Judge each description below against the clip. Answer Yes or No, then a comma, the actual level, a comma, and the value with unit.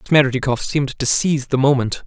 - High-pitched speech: No, low, 135 Hz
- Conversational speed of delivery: Yes, average, 175 wpm